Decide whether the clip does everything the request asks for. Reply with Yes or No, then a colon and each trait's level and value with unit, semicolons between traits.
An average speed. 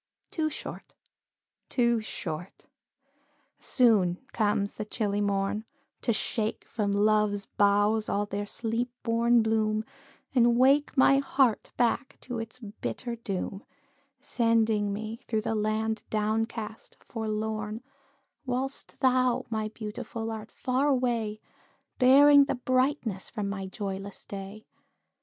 No: slow, 120 wpm